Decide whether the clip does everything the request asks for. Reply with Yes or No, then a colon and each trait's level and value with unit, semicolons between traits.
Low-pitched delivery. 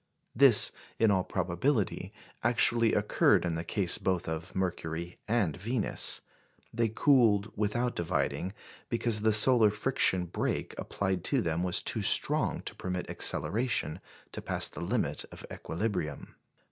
Yes: low, 100 Hz